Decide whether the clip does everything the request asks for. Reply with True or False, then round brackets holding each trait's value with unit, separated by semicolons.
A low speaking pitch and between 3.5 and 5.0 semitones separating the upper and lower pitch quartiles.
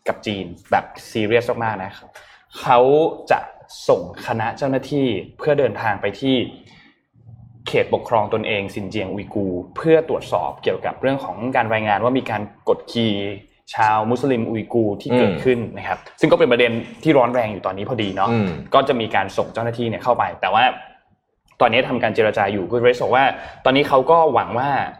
True (115 Hz; 4.2 semitones)